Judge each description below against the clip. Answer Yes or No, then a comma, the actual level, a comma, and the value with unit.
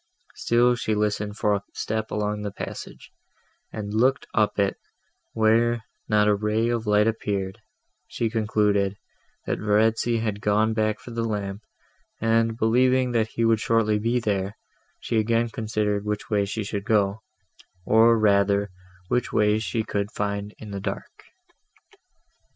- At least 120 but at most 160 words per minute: Yes, average, 150 wpm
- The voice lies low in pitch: Yes, low, 110 Hz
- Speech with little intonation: Yes, narrow, 1.7 semitones